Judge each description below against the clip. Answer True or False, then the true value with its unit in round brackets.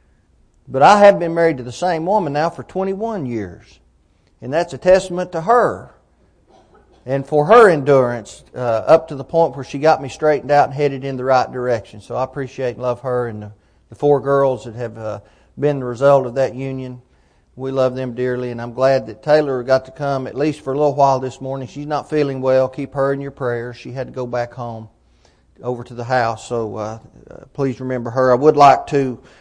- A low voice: True (130 Hz)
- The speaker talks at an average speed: False (220 wpm)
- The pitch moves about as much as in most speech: True (3.0 semitones)